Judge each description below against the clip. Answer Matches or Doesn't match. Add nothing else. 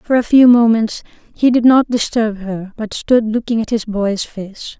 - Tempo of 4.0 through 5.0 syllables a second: Matches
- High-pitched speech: Matches